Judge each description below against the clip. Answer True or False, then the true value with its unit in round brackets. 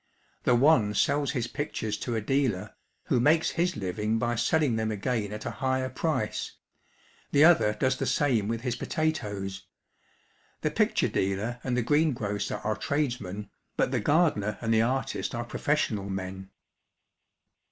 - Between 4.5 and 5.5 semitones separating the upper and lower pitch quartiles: True (4.8 semitones)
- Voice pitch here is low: True (120 Hz)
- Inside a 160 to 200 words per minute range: False (150 wpm)